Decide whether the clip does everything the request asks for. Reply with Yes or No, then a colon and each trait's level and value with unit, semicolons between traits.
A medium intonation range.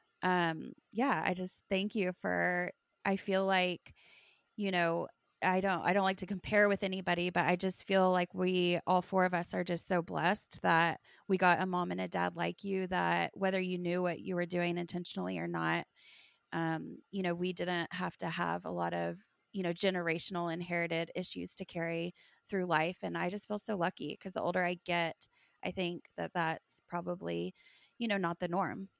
No: narrow, 1.9 semitones